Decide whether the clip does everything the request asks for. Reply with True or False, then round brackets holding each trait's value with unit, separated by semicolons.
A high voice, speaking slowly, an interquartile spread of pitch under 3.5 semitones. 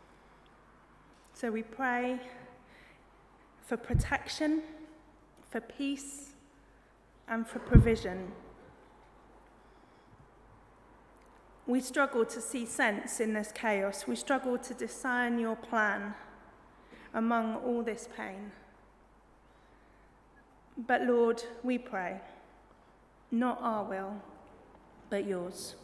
True (235 Hz; 85 wpm; 2.4 semitones)